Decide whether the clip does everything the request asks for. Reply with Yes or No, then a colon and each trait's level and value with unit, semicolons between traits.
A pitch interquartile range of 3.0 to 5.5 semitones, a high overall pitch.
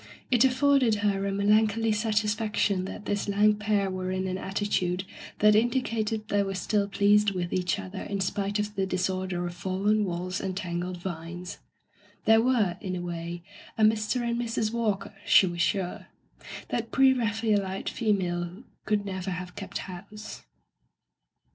No: narrow, 2.6 semitones; high, 200 Hz